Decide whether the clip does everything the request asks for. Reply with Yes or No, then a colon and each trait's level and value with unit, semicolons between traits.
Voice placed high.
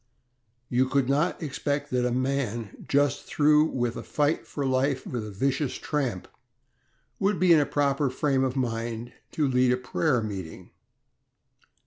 No: low, 135 Hz